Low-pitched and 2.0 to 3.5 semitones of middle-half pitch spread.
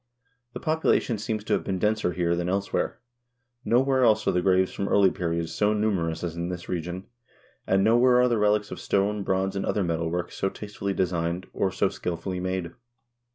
Yes: very low, 95 Hz; average, 3.0 semitones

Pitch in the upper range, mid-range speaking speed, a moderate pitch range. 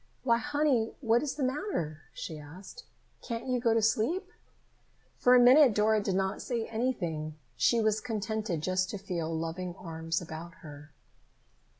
No: high, 215 Hz; average, 160 wpm; wide, 6.8 semitones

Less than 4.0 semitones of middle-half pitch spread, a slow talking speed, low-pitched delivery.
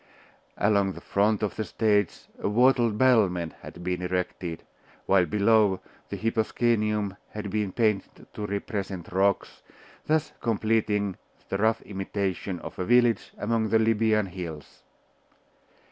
Yes: narrow, 2.6 semitones; slow, 130 wpm; low, 105 Hz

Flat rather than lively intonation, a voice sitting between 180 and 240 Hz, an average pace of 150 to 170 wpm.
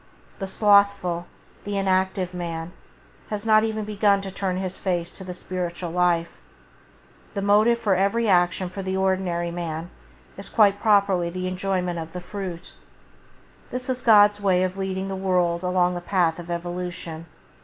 Yes: narrow, 2.3 semitones; medium, 185 Hz; average, 155 wpm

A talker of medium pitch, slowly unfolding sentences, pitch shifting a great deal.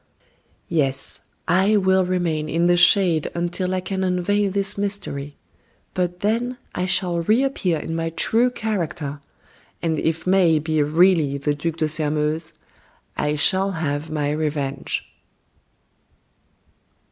No: medium, 170 Hz; slow, 125 wpm; average, 3.7 semitones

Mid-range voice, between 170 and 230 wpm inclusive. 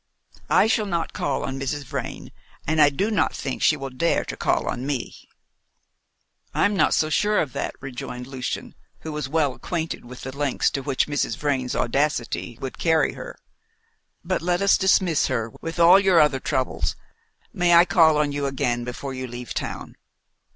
Yes: medium, 145 Hz; average, 180 wpm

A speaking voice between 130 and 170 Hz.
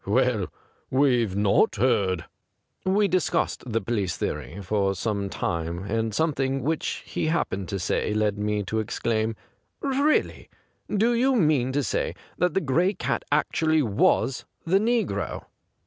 No: low, 120 Hz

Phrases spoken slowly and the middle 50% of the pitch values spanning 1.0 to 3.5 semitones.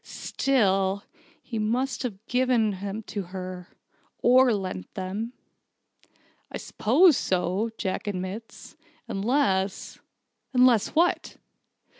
No: slow, 100 wpm; average, 4.7 semitones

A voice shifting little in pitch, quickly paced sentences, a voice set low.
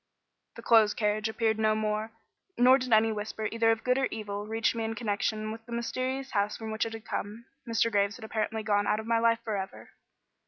No: narrow, 1.3 semitones; fast, 225 wpm; high, 220 Hz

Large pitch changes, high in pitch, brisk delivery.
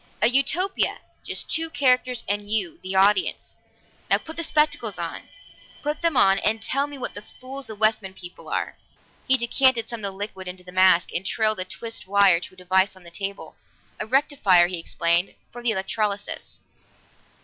No: wide, 5.7 semitones; high, 215 Hz; average, 180 wpm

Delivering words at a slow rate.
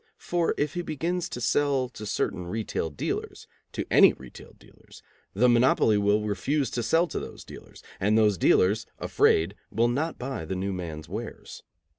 No: average, 170 wpm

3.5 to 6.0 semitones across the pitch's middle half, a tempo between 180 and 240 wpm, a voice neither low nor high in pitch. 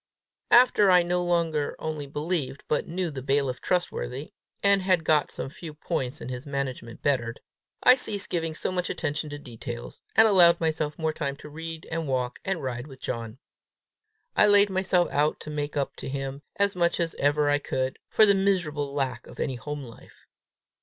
Yes: average, 4.3 semitones; average, 185 wpm; medium, 150 Hz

